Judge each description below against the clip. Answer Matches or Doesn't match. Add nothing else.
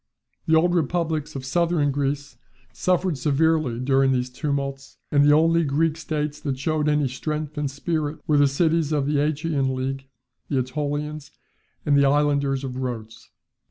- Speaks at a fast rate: Doesn't match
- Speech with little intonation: Matches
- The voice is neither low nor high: Matches